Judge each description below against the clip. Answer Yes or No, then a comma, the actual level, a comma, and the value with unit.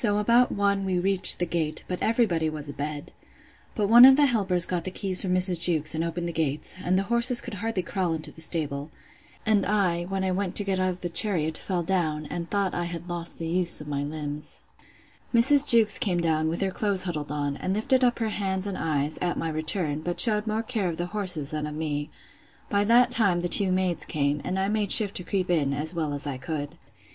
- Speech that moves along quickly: Yes, fast, 240 wpm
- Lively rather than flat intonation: No, average, 4.3 semitones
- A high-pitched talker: No, medium, 180 Hz